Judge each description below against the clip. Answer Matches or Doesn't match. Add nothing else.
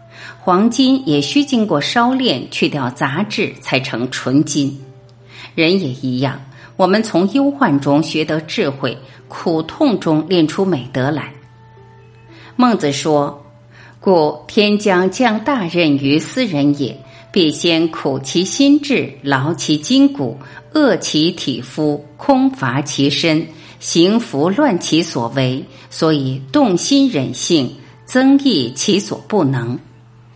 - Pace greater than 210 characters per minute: Doesn't match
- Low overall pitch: Doesn't match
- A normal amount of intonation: Doesn't match